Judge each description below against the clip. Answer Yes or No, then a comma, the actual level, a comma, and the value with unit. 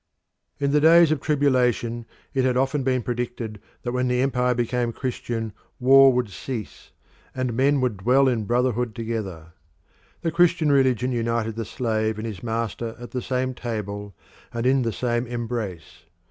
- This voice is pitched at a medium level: No, low, 120 Hz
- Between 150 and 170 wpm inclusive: Yes, average, 160 wpm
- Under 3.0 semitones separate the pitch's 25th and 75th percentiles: Yes, narrow, 2.4 semitones